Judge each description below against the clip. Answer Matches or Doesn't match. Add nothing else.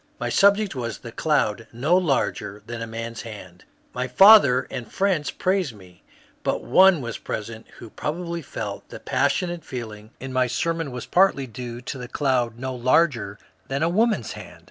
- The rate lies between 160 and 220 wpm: Matches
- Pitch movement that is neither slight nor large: Doesn't match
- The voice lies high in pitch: Doesn't match